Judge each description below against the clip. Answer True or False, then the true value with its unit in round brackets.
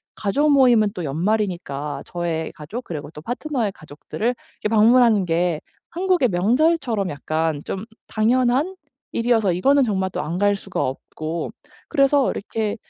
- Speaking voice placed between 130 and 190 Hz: False (205 Hz)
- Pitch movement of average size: False (6.6 semitones)